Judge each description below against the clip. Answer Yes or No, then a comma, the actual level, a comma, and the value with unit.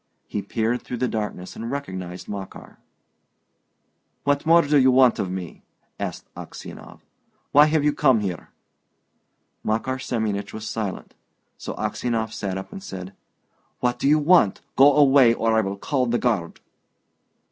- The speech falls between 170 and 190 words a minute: No, average, 150 wpm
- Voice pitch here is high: No, low, 115 Hz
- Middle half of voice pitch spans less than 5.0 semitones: No, wide, 5.4 semitones